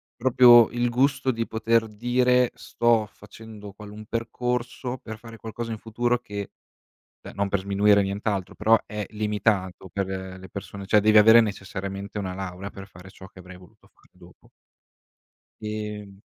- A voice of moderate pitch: No, low, 105 Hz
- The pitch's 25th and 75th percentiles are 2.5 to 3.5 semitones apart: Yes, average, 2.8 semitones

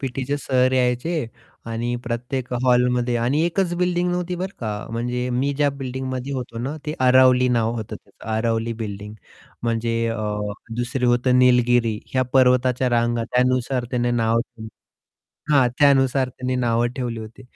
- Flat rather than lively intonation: Yes, narrow, 1.9 semitones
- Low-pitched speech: Yes, low, 125 Hz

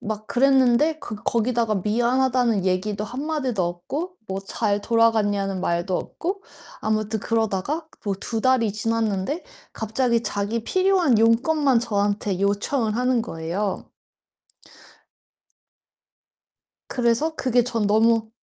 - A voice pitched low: No, high, 225 Hz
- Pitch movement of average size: Yes, average, 3.8 semitones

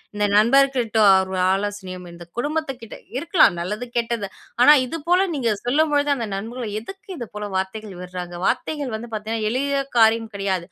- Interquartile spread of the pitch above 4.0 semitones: Yes, average, 5.2 semitones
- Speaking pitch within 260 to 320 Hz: No, high, 225 Hz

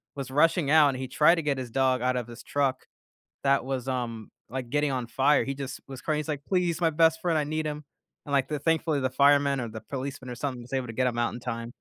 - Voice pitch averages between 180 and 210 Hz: No, low, 135 Hz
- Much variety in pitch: No, average, 2.8 semitones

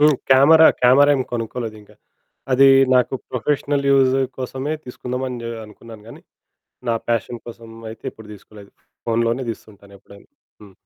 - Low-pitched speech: Yes, low, 120 Hz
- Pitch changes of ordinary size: Yes, average, 3.1 semitones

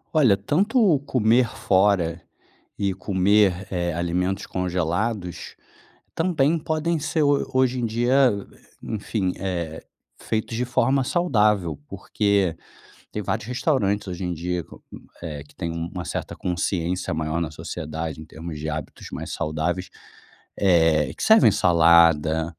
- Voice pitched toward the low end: Yes, very low, 95 Hz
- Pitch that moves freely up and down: Yes, wide, 5.8 semitones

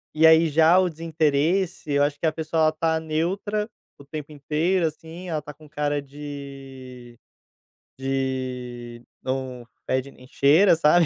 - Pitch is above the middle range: No, medium, 150 Hz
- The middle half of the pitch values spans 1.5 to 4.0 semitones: Yes, average, 3.2 semitones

